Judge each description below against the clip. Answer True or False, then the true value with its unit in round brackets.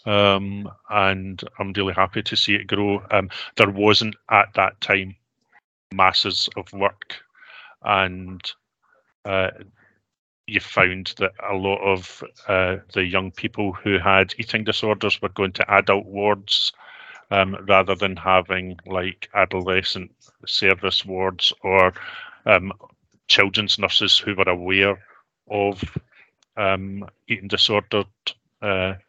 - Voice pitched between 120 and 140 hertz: False (100 Hz)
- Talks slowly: True (120 wpm)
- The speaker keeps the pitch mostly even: True (1.4 semitones)